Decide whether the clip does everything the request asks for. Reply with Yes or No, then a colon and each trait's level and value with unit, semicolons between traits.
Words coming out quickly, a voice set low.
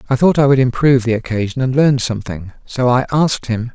Yes: fast, 225 wpm; low, 125 Hz